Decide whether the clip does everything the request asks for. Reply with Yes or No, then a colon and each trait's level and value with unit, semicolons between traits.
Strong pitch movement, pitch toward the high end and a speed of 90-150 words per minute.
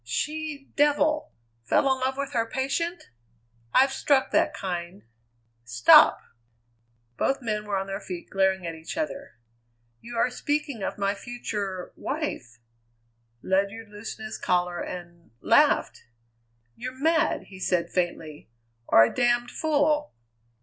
Yes: wide, 7.4 semitones; high, 220 Hz; slow, 135 wpm